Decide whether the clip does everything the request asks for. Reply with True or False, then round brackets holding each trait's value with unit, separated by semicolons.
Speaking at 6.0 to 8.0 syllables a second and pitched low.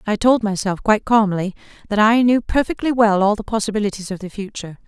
False (6.2 syllables/s; 210 Hz)